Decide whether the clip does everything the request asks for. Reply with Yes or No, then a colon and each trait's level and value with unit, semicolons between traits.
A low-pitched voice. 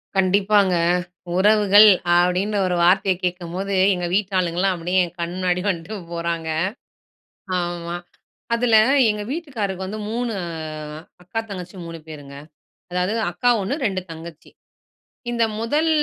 No: medium, 185 Hz